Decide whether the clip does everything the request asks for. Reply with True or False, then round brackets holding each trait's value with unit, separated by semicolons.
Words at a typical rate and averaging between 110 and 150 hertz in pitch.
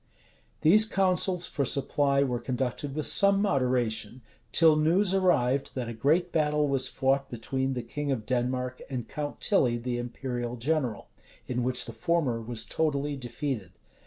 True (155 wpm; 135 Hz)